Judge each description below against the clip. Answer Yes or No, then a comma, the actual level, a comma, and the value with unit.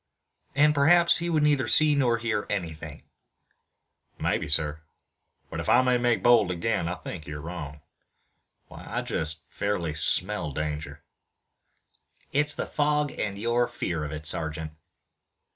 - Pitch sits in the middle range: No, low, 100 Hz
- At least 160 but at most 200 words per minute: No, average, 145 wpm